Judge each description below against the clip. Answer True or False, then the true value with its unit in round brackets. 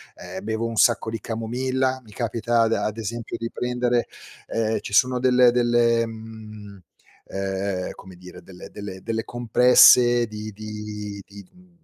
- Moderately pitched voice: False (115 Hz)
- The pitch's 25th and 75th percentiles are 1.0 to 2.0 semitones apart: False (2.6 semitones)